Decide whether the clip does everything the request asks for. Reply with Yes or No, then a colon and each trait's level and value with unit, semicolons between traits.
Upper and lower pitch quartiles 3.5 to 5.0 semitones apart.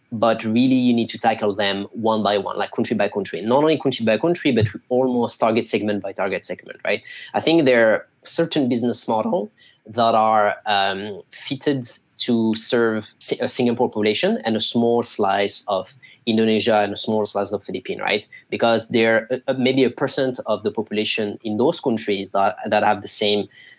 No: average, 2.8 semitones